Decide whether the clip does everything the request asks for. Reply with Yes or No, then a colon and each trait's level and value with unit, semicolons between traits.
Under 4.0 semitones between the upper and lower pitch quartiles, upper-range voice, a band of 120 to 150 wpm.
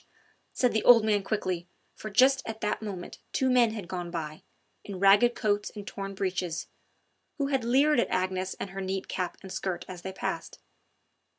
No: average, 3.6 semitones; high, 200 Hz; average, 185 wpm